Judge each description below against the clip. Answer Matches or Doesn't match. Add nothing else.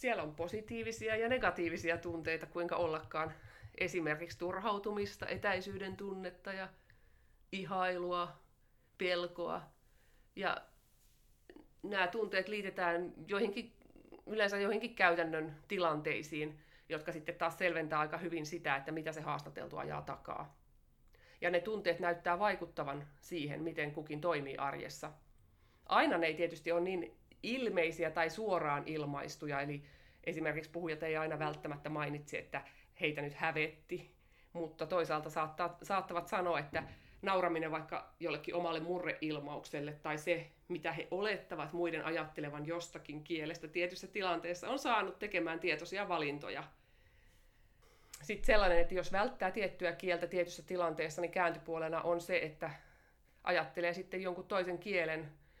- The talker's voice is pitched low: Doesn't match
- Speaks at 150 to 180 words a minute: Doesn't match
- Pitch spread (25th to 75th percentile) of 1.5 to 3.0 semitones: Matches